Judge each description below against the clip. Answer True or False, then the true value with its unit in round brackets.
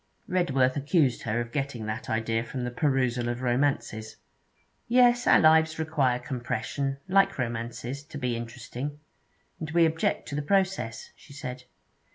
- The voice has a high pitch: False (135 Hz)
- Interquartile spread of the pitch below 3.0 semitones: False (4.8 semitones)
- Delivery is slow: False (150 wpm)